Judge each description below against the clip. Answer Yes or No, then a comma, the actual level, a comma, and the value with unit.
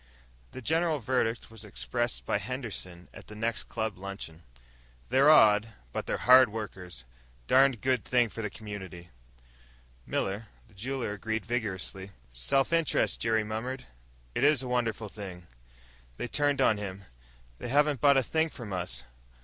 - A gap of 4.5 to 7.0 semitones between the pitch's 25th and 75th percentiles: Yes, average, 4.9 semitones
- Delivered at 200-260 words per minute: No, average, 150 wpm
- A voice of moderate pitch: No, low, 110 Hz